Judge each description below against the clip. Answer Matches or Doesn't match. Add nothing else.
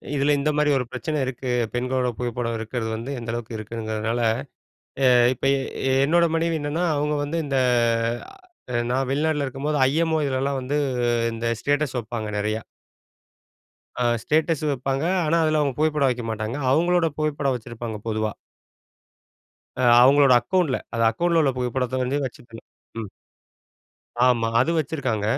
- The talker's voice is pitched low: Matches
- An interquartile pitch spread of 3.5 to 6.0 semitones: Matches